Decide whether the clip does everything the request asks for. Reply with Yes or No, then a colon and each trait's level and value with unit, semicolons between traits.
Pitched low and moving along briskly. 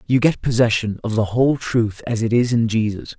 Yes: low, 115 Hz; fast, 225 wpm